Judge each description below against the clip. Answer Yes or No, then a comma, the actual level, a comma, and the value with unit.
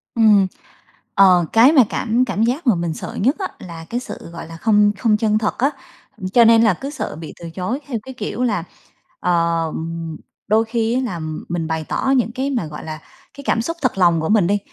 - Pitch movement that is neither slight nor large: No, wide, 6.1 semitones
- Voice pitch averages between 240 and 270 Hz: No, high, 210 Hz